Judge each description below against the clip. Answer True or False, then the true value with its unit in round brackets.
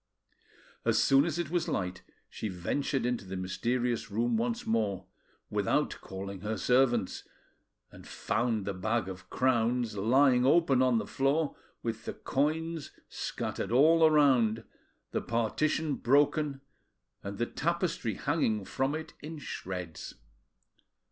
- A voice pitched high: False (120 Hz)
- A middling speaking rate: False (130 wpm)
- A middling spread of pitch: True (5.0 semitones)